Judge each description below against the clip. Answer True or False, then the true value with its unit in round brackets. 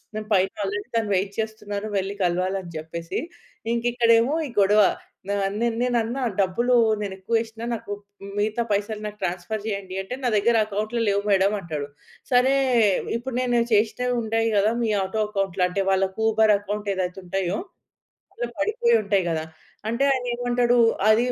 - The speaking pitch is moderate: False (210 Hz)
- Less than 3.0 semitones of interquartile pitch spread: False (3.3 semitones)